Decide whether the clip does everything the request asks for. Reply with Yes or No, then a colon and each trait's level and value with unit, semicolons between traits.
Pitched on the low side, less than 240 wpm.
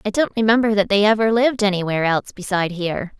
No: high, 205 Hz; fast, 205 wpm